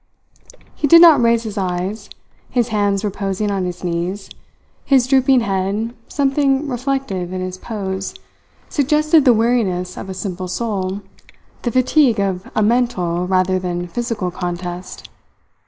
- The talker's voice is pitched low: No, high, 205 Hz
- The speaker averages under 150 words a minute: Yes, average, 140 wpm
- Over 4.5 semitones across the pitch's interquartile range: Yes, average, 5.0 semitones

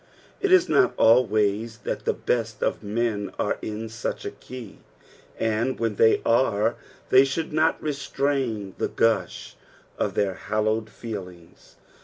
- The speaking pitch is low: Yes, low, 115 Hz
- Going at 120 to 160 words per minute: Yes, average, 140 wpm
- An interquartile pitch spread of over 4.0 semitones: No, average, 3.5 semitones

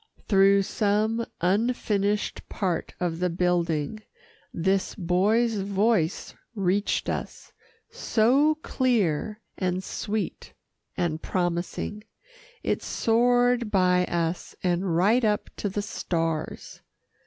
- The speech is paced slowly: Yes, slow, 95 wpm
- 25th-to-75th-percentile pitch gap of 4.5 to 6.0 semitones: No, average, 3.6 semitones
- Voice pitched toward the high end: Yes, high, 195 Hz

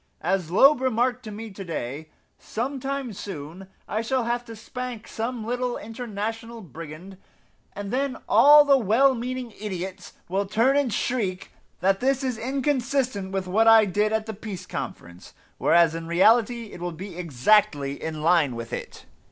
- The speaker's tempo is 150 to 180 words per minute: Yes, average, 165 wpm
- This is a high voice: Yes, high, 215 Hz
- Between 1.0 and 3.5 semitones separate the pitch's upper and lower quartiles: No, average, 5.2 semitones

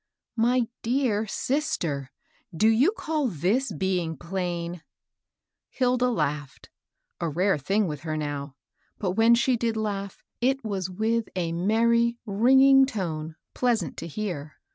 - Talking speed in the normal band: Yes, average, 155 wpm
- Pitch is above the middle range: Yes, high, 205 Hz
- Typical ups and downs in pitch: No, wide, 6.0 semitones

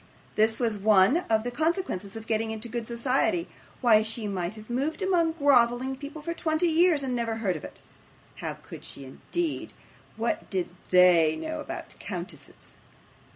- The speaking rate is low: No, average, 165 wpm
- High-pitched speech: Yes, high, 235 Hz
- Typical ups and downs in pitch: No, wide, 6.3 semitones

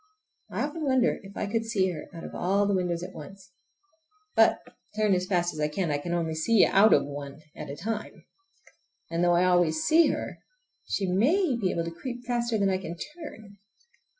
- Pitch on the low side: No, high, 190 Hz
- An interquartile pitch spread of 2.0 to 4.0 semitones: No, average, 4.7 semitones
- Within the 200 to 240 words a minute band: Yes, fast, 205 wpm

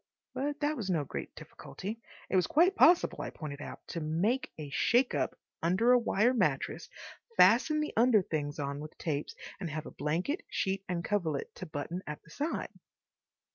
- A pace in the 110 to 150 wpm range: No, average, 180 wpm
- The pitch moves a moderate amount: No, wide, 8.2 semitones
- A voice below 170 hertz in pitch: No, medium, 185 Hz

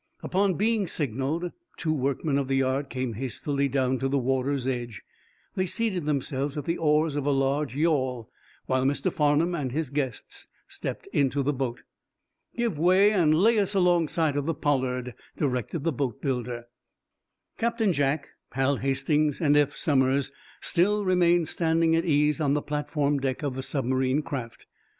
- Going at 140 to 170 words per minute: Yes, average, 160 wpm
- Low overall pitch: No, medium, 145 Hz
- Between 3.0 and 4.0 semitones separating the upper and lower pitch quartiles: Yes, average, 3.6 semitones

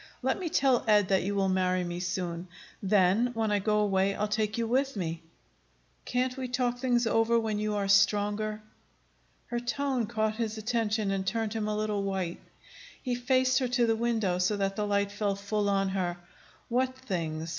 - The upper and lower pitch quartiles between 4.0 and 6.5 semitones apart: No, average, 3.3 semitones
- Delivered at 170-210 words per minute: Yes, average, 190 wpm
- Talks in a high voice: Yes, high, 210 Hz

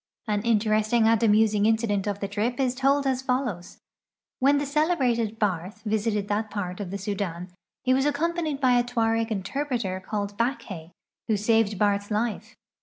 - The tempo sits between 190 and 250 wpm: No, average, 170 wpm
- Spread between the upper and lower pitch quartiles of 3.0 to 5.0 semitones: Yes, average, 3.6 semitones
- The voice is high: Yes, high, 220 Hz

